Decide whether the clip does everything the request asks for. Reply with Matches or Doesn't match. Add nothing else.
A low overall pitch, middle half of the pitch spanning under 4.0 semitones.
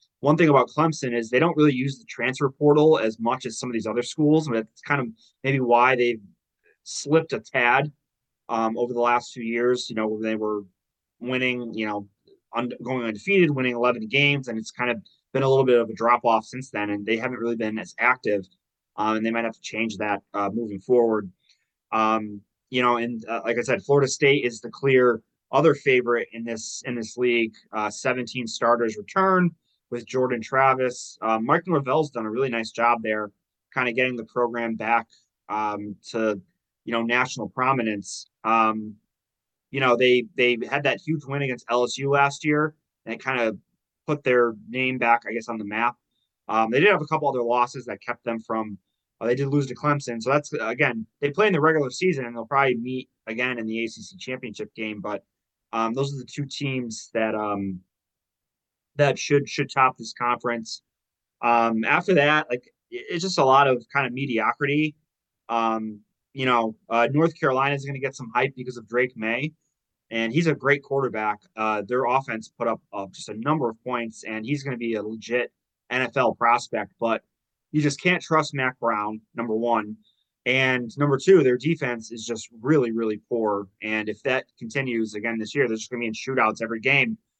Matches